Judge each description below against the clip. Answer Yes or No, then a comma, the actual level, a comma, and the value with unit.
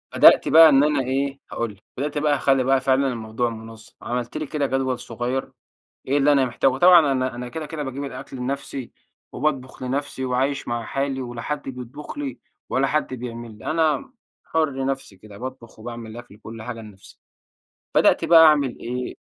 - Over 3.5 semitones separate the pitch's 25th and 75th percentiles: No, average, 2.9 semitones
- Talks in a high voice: No, low, 130 Hz